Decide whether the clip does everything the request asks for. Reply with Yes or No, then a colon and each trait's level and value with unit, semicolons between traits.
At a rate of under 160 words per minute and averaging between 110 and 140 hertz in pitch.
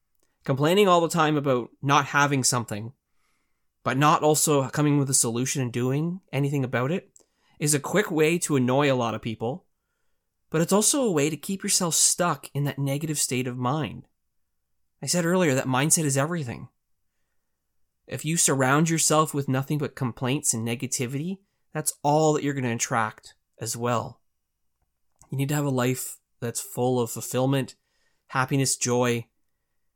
No: average, 165 wpm; low, 135 Hz